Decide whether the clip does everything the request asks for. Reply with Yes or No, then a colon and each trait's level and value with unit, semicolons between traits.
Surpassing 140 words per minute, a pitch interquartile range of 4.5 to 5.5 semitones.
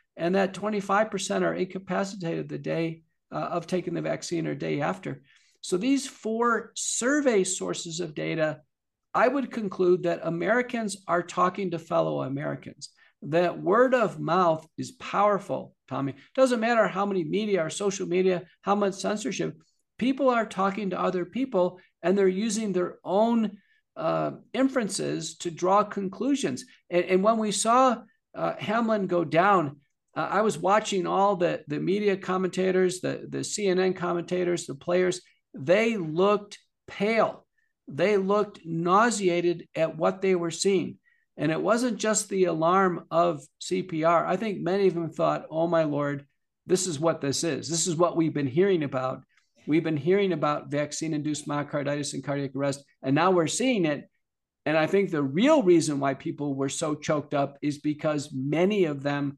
No: average, 160 wpm; average, 3.9 semitones